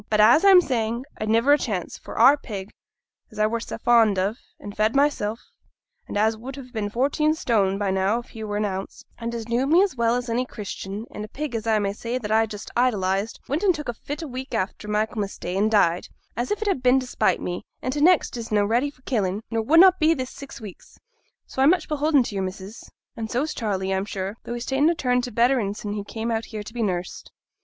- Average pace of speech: No, fast, 250 wpm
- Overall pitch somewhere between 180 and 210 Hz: No, high, 230 Hz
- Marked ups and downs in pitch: No, average, 4.1 semitones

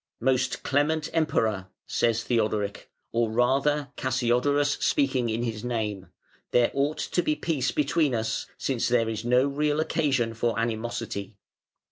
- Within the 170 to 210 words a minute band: No, slow, 135 wpm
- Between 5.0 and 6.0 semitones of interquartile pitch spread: No, average, 4.0 semitones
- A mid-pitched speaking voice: No, low, 125 Hz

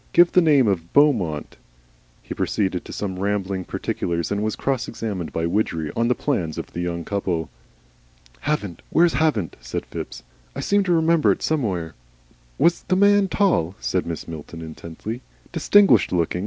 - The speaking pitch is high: No, low, 100 Hz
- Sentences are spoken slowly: No, average, 165 wpm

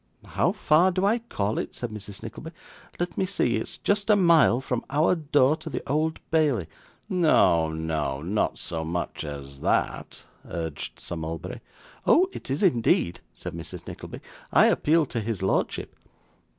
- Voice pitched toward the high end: No, low, 125 Hz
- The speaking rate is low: No, average, 165 wpm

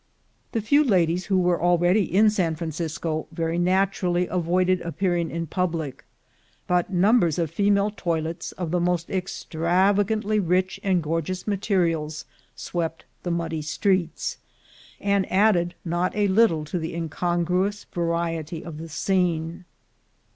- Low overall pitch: No, medium, 175 Hz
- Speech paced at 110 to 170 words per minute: Yes, slow, 135 wpm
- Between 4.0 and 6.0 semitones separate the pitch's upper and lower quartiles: No, narrow, 2.4 semitones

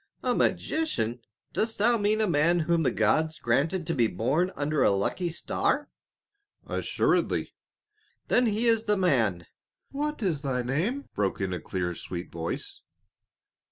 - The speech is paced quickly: No, average, 150 wpm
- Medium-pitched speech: Yes, medium, 155 Hz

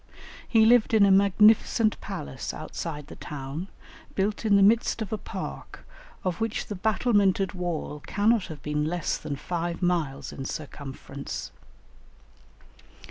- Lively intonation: Yes, wide, 5.8 semitones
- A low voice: No, medium, 185 Hz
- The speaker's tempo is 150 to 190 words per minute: No, slow, 135 wpm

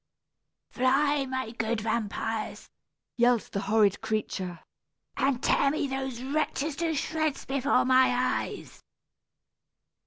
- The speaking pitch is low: No, very high, 255 Hz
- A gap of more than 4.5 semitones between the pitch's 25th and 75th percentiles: No, average, 3.7 semitones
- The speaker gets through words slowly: Yes, slow, 105 wpm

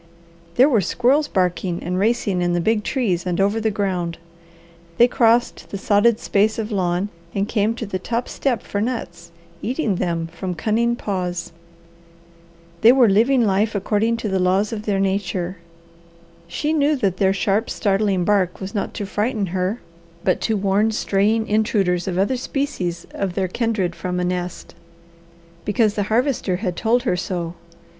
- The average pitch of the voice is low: No, high, 200 Hz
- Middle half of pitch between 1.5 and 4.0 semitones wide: Yes, average, 3.6 semitones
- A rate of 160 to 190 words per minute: Yes, average, 165 wpm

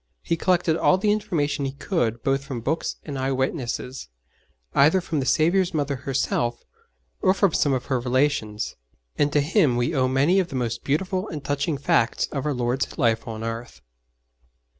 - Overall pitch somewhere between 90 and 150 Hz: Yes, medium, 140 Hz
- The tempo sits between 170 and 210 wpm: Yes, average, 180 wpm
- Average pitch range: Yes, average, 4.5 semitones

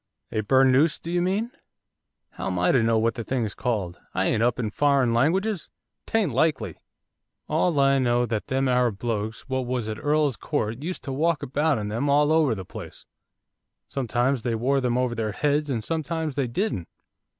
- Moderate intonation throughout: Yes, average, 4.4 semitones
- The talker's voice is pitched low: Yes, low, 130 Hz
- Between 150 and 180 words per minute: No, average, 190 wpm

